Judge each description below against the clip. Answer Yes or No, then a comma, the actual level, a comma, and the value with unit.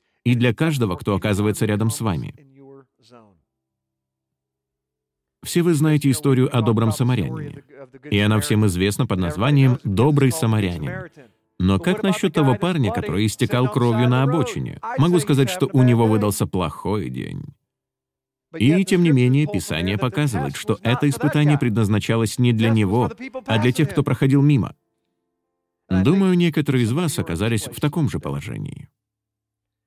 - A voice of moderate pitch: No, low, 120 Hz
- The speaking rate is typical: Yes, average, 140 wpm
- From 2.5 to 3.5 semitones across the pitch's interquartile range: No, wide, 5.5 semitones